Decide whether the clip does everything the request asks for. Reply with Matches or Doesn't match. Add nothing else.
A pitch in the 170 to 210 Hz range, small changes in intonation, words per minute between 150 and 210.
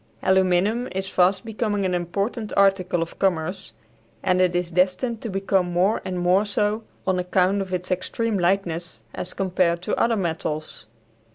Matches